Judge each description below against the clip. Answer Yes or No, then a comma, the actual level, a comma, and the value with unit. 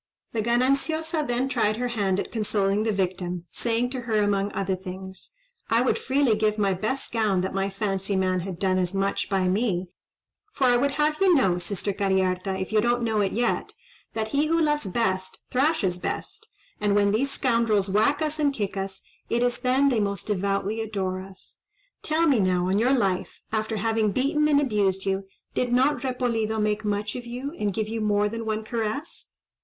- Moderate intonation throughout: Yes, average, 4.3 semitones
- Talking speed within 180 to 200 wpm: Yes, average, 195 wpm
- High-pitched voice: Yes, high, 215 Hz